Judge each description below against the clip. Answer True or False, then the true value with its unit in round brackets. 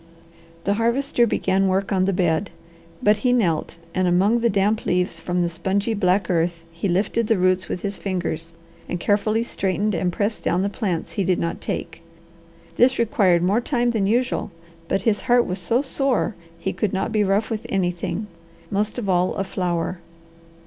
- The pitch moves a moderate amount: True (3.4 semitones)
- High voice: True (195 Hz)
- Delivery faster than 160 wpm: True (185 wpm)